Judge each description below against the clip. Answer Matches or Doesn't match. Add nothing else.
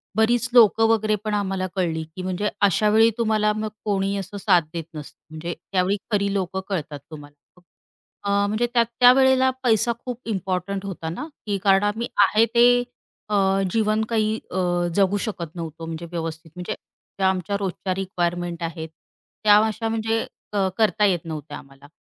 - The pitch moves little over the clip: Doesn't match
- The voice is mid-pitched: Doesn't match